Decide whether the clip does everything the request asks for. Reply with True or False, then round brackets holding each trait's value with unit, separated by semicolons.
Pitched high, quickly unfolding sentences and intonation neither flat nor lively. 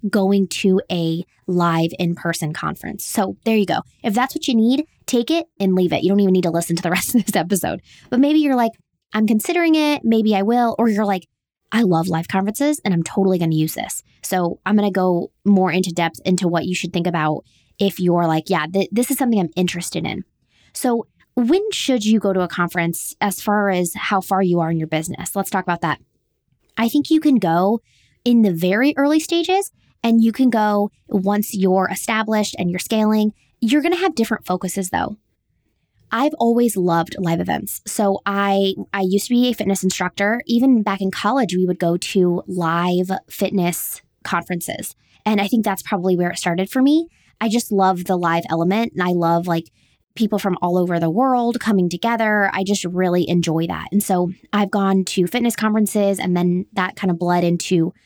True (195 Hz; 210 wpm; 4.1 semitones)